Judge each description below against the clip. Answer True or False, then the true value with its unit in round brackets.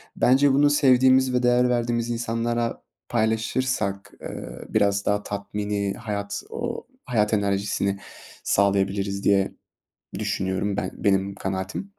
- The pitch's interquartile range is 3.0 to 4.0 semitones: True (3.7 semitones)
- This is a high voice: False (105 Hz)